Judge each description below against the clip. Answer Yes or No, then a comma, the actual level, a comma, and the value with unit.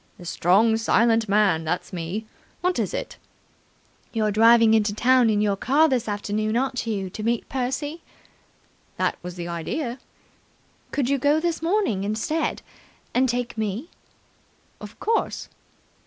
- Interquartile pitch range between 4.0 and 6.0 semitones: Yes, average, 4.3 semitones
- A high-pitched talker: Yes, high, 225 Hz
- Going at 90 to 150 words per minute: Yes, average, 140 wpm